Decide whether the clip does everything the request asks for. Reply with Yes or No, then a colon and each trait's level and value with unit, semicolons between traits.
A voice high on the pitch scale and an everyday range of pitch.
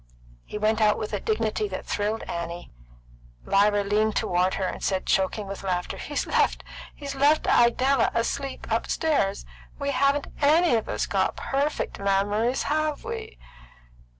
No: high, 220 Hz; wide, 6.0 semitones